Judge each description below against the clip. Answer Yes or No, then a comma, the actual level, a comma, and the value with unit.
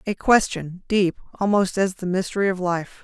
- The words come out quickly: No, average, 180 wpm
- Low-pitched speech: No, high, 190 Hz